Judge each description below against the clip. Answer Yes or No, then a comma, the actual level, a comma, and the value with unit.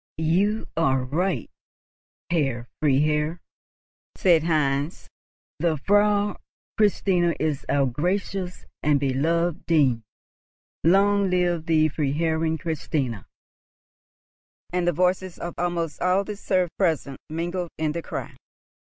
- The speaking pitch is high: No, medium, 165 Hz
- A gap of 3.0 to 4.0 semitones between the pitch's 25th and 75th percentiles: Yes, average, 3.3 semitones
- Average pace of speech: No, slow, 110 wpm